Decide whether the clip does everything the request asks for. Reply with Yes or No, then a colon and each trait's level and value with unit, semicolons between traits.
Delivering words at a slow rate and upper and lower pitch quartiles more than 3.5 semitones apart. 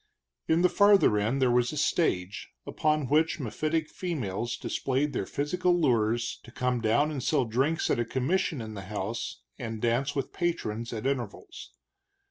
No: average, 170 wpm; average, 5.1 semitones